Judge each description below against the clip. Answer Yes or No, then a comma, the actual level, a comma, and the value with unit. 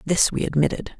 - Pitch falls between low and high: Yes, medium, 165 Hz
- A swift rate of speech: No, average, 180 wpm